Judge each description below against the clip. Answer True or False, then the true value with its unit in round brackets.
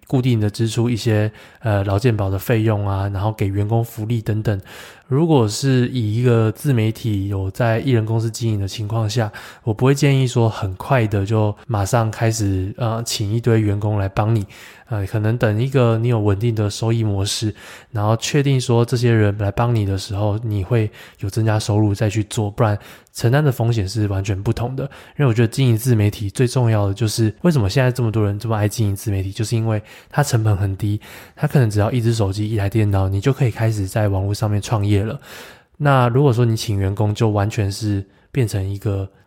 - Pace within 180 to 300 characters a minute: False (315 characters per minute)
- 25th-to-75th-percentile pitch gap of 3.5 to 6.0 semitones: False (2.5 semitones)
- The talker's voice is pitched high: False (110 Hz)